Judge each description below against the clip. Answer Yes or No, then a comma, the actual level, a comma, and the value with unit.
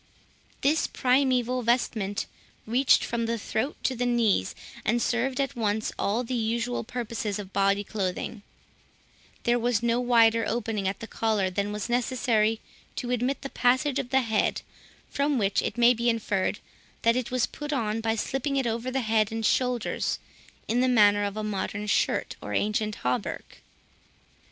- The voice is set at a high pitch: Yes, high, 230 Hz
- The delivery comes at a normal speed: Yes, average, 165 wpm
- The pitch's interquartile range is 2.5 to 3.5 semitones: Yes, average, 2.8 semitones